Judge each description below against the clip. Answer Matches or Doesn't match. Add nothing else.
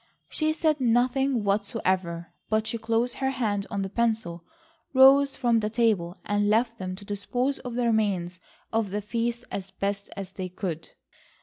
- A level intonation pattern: Doesn't match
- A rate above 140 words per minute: Matches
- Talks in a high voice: Matches